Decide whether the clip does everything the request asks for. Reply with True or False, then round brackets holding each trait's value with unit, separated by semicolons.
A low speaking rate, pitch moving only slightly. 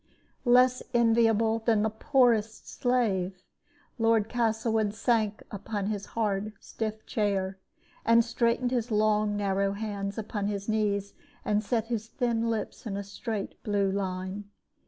True (130 wpm; 2.2 semitones)